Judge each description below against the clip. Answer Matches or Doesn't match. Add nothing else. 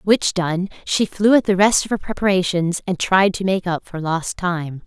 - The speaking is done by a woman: Matches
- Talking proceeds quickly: Matches